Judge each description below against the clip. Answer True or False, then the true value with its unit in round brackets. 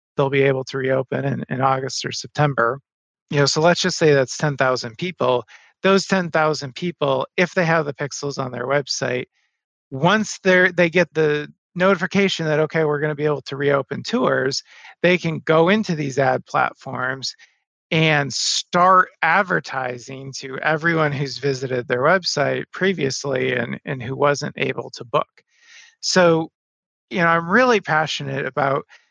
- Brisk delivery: False (165 wpm)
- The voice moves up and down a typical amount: True (4.2 semitones)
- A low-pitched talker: False (150 Hz)